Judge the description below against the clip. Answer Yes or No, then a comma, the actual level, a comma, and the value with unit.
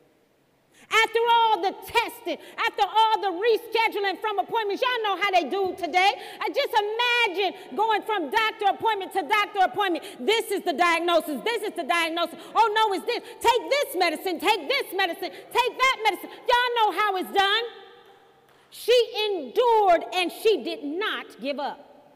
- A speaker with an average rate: Yes, average, 160 wpm